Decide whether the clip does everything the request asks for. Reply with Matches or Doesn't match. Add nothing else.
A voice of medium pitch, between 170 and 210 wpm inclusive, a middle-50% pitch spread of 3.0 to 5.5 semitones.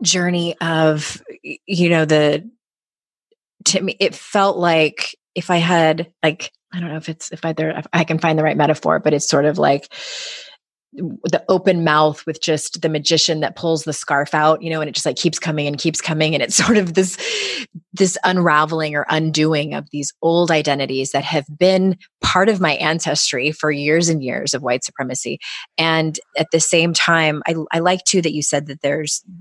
Doesn't match